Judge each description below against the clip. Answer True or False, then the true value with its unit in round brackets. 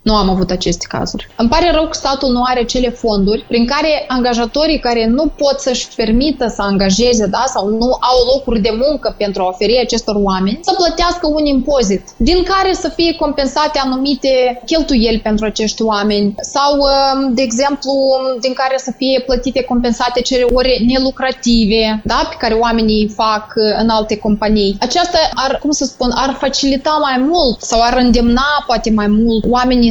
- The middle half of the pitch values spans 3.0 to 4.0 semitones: True (3.7 semitones)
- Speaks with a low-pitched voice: False (250 Hz)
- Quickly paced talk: True (175 wpm)